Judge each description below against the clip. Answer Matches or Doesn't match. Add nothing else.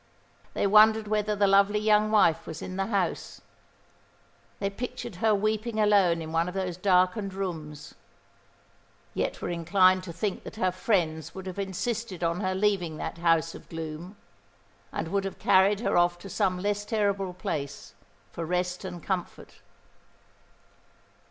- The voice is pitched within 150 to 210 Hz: Matches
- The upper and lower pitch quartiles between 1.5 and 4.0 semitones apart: Matches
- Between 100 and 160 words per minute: Matches